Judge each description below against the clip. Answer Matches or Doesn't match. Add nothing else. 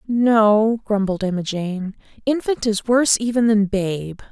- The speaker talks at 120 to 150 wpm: Matches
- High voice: Matches